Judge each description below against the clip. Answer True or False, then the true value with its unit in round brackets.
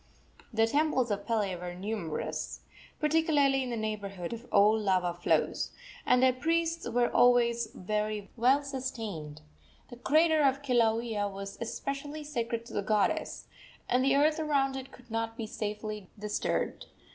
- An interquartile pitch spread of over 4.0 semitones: True (4.4 semitones)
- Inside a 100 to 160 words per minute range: True (145 wpm)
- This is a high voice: True (235 Hz)